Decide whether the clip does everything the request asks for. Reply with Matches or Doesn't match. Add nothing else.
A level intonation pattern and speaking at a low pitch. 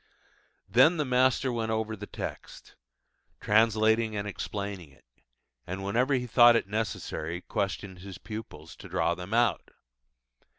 Doesn't match